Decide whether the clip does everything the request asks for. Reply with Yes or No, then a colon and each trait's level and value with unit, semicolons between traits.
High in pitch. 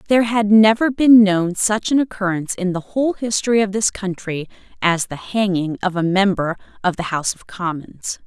Yes: high, 200 Hz